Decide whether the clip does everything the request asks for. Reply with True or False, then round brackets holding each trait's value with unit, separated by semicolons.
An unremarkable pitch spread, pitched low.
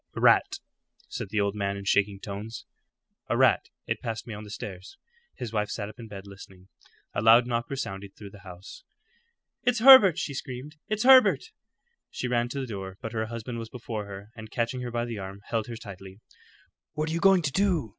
True (4.2 semitones; 115 Hz)